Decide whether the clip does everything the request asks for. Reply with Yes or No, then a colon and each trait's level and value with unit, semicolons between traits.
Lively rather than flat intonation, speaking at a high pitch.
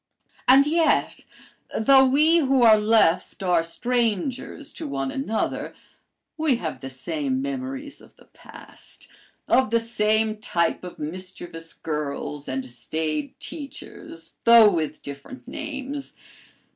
Yes: wide, 8.6 semitones; high, 220 Hz